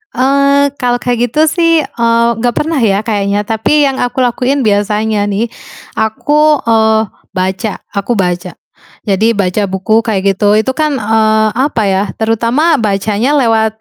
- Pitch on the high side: Yes, high, 225 Hz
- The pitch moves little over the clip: No, average, 3.9 semitones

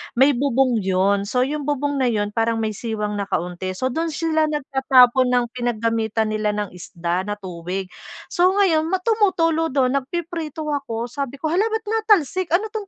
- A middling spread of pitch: No, wide, 7.0 semitones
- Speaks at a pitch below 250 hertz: No, very high, 260 Hz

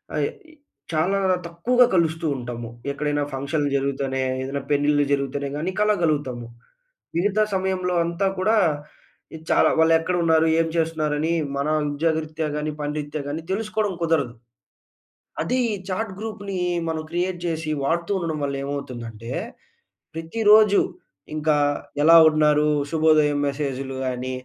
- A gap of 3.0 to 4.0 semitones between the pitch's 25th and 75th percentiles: Yes, average, 3.7 semitones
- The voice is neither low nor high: Yes, medium, 155 Hz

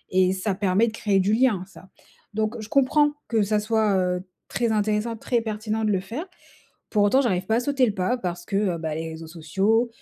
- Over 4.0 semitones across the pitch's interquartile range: No, average, 3.5 semitones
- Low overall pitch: No, high, 210 Hz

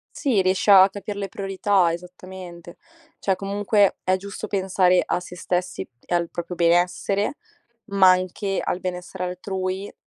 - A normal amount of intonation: No, narrow, 1.7 semitones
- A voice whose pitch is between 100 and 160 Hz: No, medium, 185 Hz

